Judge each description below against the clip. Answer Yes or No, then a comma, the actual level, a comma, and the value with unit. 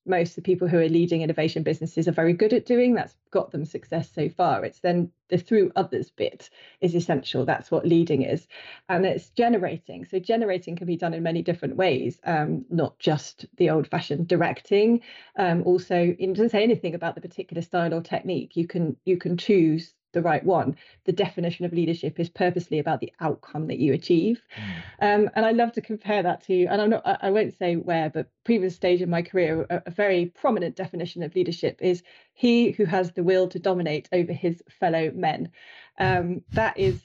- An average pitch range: No, narrow, 2.2 semitones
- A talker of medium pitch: Yes, medium, 175 Hz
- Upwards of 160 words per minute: Yes, fast, 205 wpm